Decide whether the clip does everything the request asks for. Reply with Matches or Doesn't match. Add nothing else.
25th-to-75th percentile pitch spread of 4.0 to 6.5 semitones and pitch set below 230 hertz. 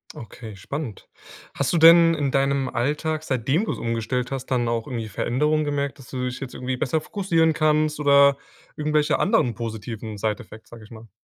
Matches